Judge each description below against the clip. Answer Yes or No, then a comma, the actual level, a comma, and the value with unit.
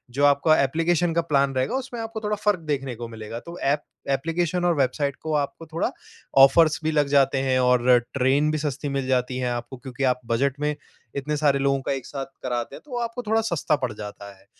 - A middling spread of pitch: Yes, average, 4.0 semitones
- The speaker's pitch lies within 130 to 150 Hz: Yes, medium, 140 Hz